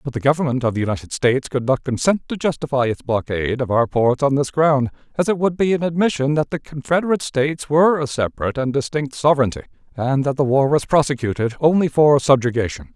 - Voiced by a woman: No, male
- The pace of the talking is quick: Yes, fast, 210 wpm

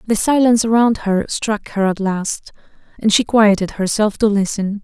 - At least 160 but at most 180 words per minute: Yes, average, 175 wpm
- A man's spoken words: No, female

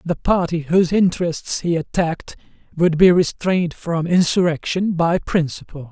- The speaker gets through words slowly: Yes, slow, 130 wpm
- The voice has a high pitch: No, medium, 170 Hz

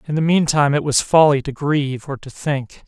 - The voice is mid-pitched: Yes, medium, 145 Hz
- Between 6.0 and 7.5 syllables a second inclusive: No, 5.5 syllables/s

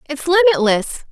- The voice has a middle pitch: No, very high, 295 Hz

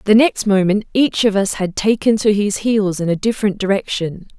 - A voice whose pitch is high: Yes, high, 205 Hz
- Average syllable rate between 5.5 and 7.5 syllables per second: No, 5.1 syllables/s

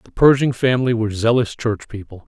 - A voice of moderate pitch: No, low, 115 Hz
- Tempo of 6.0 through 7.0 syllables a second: Yes, 6.1 syllables/s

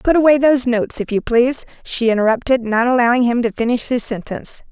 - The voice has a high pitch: Yes, high, 240 Hz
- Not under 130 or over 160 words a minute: No, fast, 205 wpm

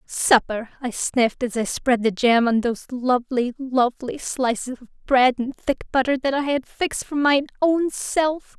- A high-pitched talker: Yes, very high, 255 Hz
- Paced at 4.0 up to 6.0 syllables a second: Yes, 4.7 syllables/s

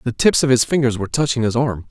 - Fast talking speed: Yes, fast, 285 wpm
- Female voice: No, male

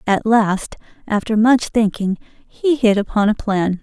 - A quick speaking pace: No, average, 155 wpm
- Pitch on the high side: Yes, high, 215 Hz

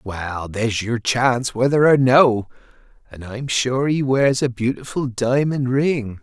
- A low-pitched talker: Yes, low, 125 Hz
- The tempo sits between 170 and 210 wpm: No, average, 155 wpm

